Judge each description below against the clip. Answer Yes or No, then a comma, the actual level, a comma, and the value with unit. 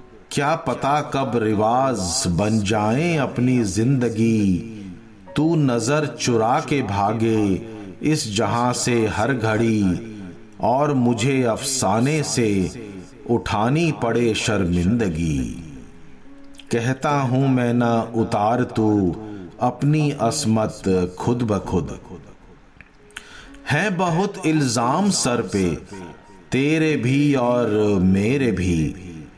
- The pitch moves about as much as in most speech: Yes, average, 4.7 semitones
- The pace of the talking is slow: Yes, slow, 95 wpm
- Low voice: Yes, low, 120 Hz